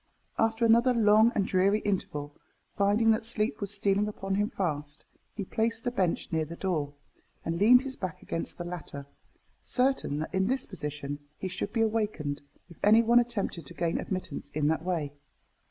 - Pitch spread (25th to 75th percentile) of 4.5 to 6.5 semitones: Yes, average, 5.2 semitones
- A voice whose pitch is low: No, high, 195 Hz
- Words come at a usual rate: Yes, average, 180 wpm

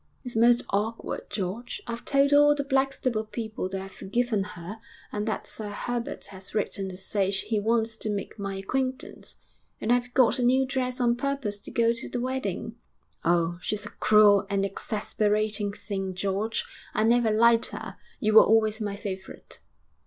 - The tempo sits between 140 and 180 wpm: Yes, average, 175 wpm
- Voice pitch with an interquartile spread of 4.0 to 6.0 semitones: No, average, 3.2 semitones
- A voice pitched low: No, high, 220 Hz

